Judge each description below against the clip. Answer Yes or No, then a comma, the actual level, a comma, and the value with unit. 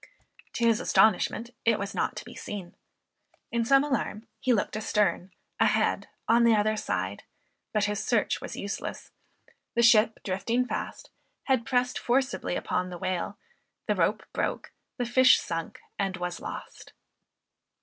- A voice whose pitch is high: Yes, high, 215 Hz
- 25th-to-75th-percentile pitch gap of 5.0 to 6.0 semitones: No, average, 3.5 semitones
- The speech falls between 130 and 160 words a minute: Yes, average, 155 wpm